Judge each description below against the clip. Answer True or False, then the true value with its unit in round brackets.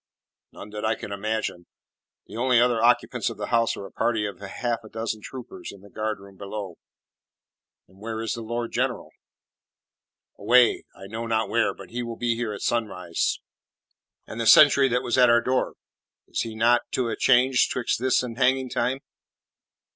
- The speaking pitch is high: False (115 Hz)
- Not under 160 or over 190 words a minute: True (180 wpm)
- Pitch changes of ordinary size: False (2.2 semitones)